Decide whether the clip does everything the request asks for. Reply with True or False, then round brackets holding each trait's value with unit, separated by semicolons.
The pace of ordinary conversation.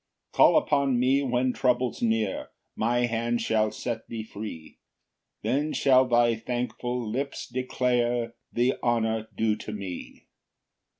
False (130 wpm)